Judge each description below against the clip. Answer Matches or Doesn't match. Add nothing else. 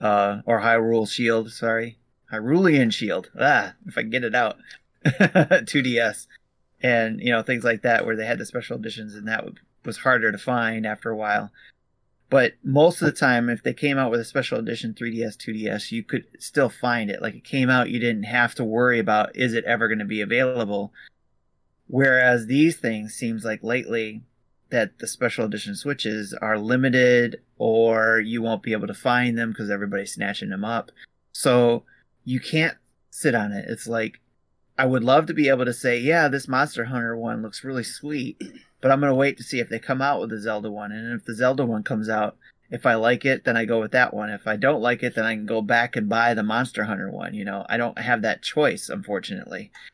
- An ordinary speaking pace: Doesn't match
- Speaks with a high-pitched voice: Doesn't match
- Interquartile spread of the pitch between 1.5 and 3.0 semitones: Matches